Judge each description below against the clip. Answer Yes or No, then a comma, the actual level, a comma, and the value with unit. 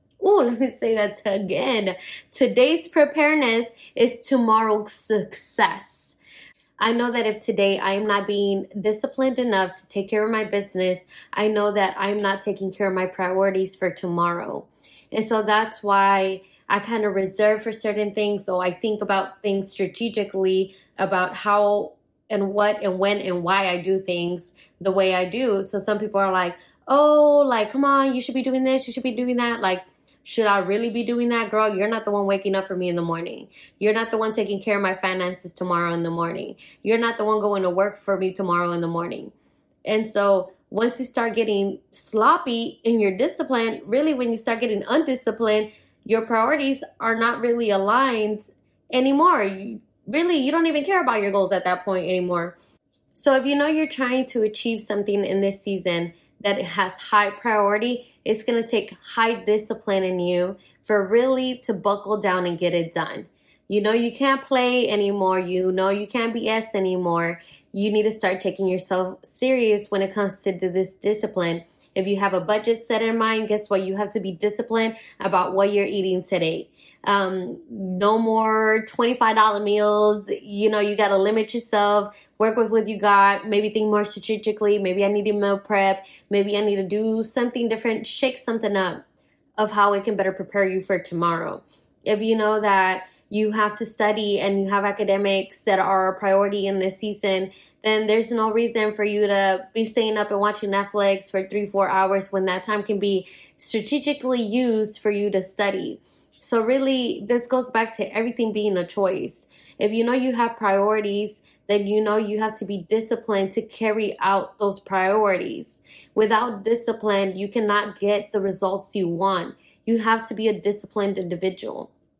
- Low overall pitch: No, high, 210 Hz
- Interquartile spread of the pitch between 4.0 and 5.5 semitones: No, narrow, 2.6 semitones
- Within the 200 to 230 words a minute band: No, average, 190 wpm